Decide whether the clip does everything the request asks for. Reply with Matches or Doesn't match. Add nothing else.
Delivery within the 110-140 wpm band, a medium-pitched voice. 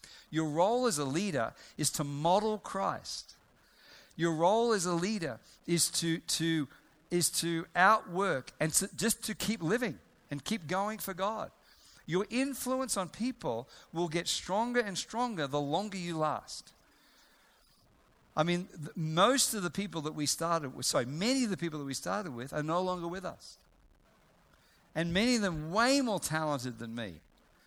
Doesn't match